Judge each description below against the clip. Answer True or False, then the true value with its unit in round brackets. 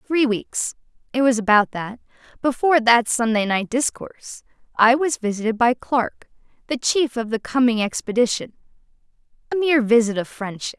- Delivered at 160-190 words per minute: False (135 wpm)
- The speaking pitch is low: False (240 Hz)